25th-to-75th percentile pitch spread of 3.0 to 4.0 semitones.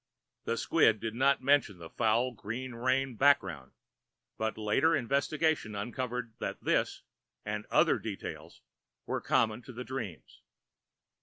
Yes: average, 3.6 semitones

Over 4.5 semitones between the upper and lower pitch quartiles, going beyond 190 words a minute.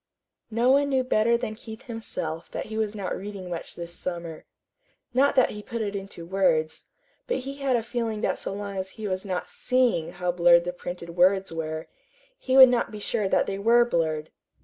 Yes: average, 5.1 semitones; fast, 205 wpm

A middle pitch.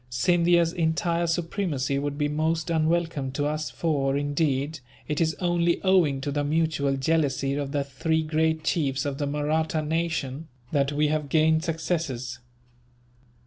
Yes: medium, 155 Hz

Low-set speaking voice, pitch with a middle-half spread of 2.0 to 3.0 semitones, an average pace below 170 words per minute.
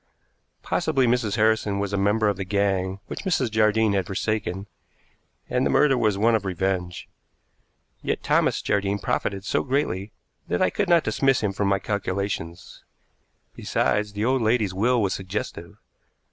Yes: low, 105 Hz; narrow, 2.5 semitones; average, 160 wpm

